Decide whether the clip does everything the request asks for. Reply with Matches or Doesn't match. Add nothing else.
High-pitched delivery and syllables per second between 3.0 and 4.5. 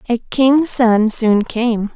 Doesn't match